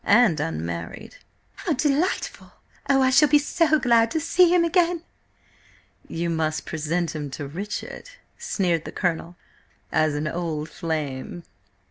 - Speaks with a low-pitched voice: No, medium, 175 Hz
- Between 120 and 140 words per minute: Yes, slow, 135 wpm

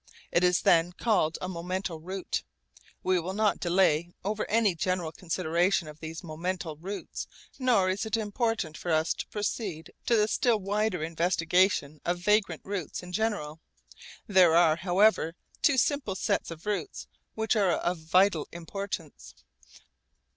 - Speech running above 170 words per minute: No, average, 145 wpm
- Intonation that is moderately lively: Yes, average, 3.7 semitones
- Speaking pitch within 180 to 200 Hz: Yes, medium, 185 Hz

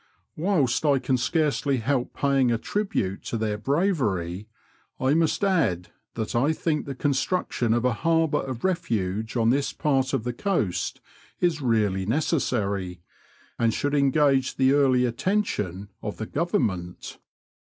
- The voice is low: Yes, low, 130 Hz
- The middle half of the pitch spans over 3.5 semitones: Yes, wide, 5.4 semitones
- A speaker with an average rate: Yes, average, 145 wpm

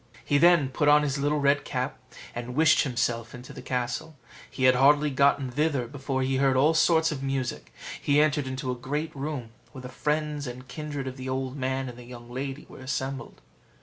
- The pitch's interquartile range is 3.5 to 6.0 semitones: No, narrow, 2.4 semitones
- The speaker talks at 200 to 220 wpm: Yes, fast, 205 wpm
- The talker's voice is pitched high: No, low, 135 Hz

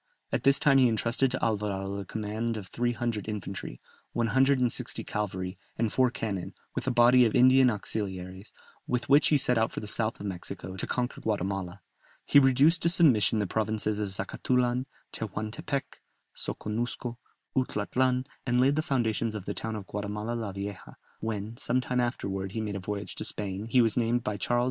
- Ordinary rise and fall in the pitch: Yes, average, 3.5 semitones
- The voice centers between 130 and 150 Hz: No, low, 110 Hz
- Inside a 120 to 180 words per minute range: No, average, 190 wpm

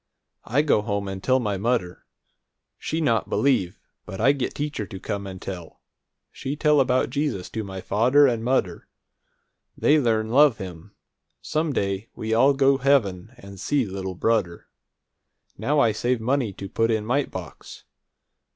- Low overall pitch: Yes, low, 115 Hz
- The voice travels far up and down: Yes, wide, 5.8 semitones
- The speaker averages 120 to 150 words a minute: No, average, 160 wpm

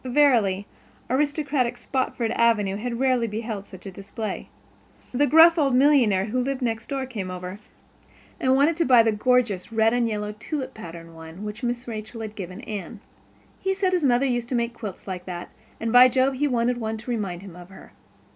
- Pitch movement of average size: Yes, average, 4.0 semitones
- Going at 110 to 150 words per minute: No, average, 195 wpm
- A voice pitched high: Yes, high, 235 Hz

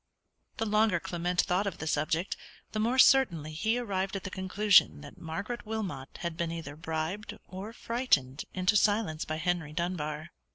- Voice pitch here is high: No, medium, 180 Hz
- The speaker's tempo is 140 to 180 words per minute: Yes, average, 165 wpm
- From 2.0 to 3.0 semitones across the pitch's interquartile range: No, average, 4.8 semitones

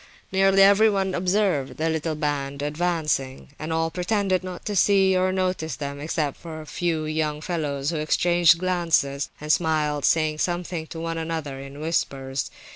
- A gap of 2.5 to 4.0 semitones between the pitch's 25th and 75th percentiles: Yes, average, 3.4 semitones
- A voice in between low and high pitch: Yes, medium, 160 Hz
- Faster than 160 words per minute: No, average, 155 wpm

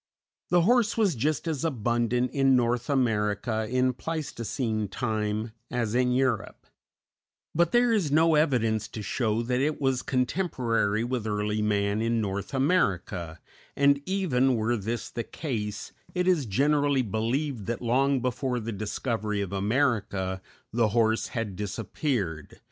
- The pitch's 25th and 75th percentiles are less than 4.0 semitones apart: No, average, 4.5 semitones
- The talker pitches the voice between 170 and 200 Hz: No, low, 120 Hz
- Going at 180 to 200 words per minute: No, average, 140 wpm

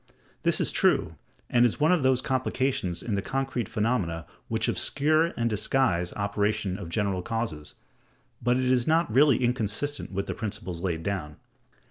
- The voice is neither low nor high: No, low, 115 Hz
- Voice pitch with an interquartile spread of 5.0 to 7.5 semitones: Yes, average, 5.3 semitones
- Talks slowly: No, average, 165 wpm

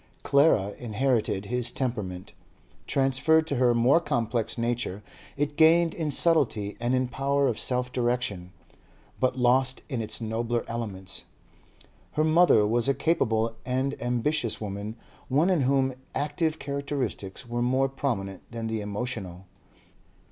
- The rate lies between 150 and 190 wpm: No, slow, 135 wpm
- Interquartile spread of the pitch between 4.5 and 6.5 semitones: No, average, 3.8 semitones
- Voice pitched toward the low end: Yes, low, 125 Hz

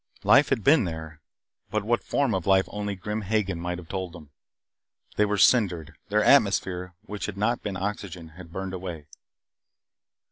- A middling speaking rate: Yes, average, 170 wpm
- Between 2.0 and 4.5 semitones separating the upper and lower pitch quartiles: Yes, average, 3.1 semitones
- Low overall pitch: Yes, very low, 95 Hz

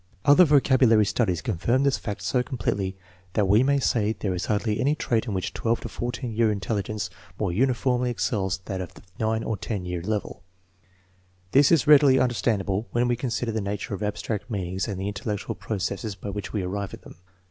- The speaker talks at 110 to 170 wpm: No, average, 195 wpm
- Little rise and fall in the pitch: No, average, 3.8 semitones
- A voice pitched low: Yes, low, 110 Hz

